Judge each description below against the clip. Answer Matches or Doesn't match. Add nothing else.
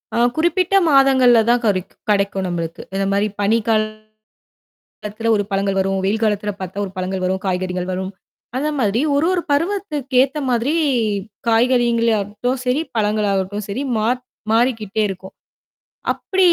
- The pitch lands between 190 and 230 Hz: Matches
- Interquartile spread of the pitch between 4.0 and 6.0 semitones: Matches